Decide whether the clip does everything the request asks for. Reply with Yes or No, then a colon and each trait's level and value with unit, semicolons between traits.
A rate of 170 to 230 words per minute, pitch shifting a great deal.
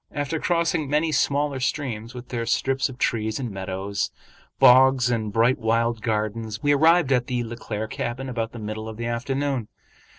No: average, 175 wpm; average, 3.5 semitones